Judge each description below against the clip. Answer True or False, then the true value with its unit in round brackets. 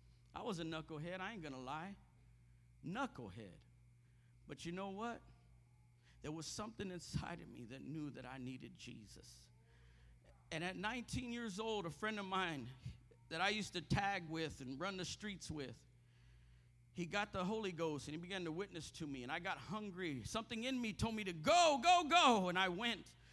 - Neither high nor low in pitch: True (160 Hz)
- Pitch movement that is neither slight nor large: False (8.6 semitones)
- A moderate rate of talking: True (190 wpm)